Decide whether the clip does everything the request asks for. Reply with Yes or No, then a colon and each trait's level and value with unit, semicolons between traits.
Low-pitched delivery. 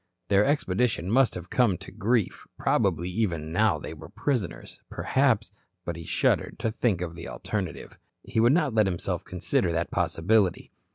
Yes: low, 100 Hz